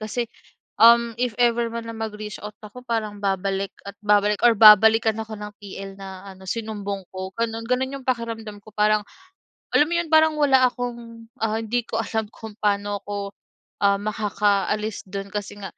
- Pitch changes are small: Yes, narrow, 2.3 semitones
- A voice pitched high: Yes, high, 215 Hz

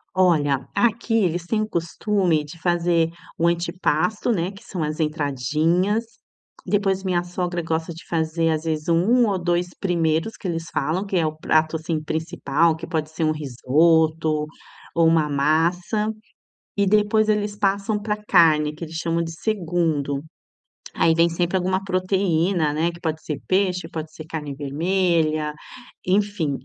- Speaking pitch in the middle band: Yes, medium, 170 Hz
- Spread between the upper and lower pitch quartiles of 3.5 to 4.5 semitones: No, average, 3.1 semitones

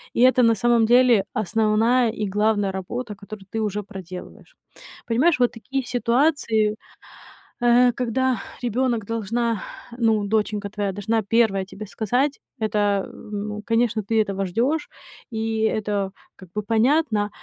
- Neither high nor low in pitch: No, high, 220 Hz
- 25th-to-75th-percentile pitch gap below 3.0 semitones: Yes, narrow, 2.6 semitones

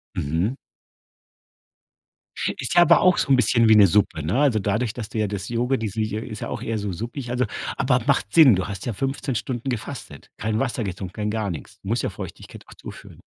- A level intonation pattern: No, average, 3.7 semitones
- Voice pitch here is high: No, low, 110 Hz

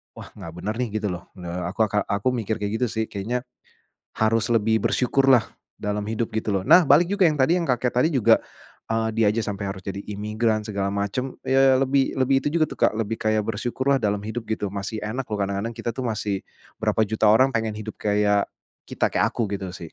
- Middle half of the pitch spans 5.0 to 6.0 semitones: No, average, 3.2 semitones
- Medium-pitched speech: No, low, 110 Hz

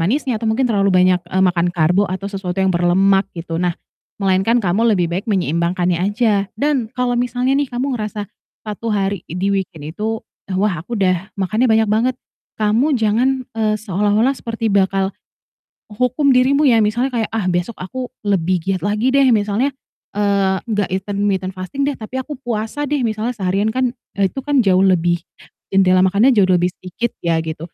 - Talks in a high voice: Yes, high, 205 Hz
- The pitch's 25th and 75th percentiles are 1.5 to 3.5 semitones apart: No, average, 4.1 semitones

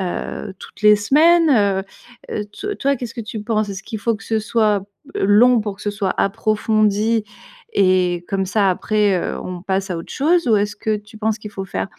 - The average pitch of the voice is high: Yes, high, 210 Hz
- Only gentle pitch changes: Yes, narrow, 2.3 semitones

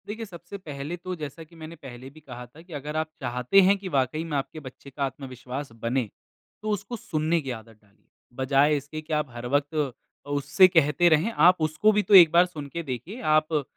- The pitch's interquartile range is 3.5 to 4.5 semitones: Yes, average, 4.1 semitones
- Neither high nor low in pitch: Yes, medium, 155 Hz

